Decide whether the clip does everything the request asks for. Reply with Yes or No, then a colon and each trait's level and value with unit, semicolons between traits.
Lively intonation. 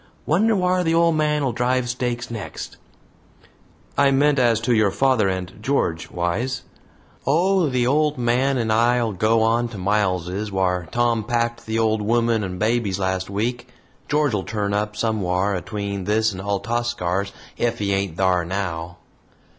No: average, 4.1 semitones